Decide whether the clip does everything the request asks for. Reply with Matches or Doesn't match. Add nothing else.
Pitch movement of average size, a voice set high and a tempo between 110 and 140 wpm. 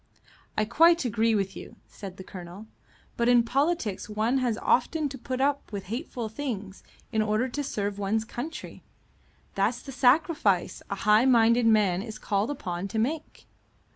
Doesn't match